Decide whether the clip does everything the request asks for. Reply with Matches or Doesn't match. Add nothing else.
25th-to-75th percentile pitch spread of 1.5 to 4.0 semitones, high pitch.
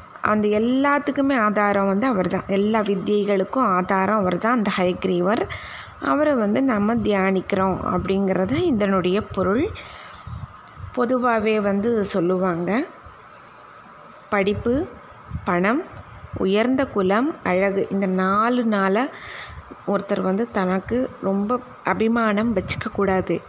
Matches